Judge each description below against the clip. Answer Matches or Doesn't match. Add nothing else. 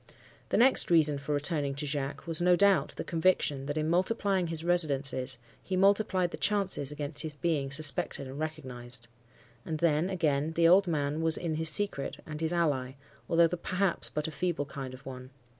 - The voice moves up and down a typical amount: Matches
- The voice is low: Doesn't match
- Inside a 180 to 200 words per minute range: Matches